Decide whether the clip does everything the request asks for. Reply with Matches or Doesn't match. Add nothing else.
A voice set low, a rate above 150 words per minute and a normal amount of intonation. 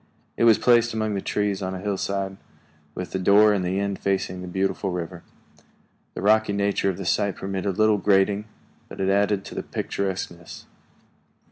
Doesn't match